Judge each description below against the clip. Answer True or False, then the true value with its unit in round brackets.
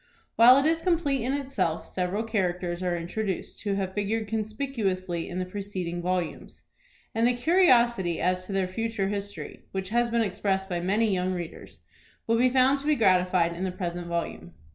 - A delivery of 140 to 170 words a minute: False (180 wpm)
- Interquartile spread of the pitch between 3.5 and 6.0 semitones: True (4.3 semitones)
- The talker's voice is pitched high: True (195 Hz)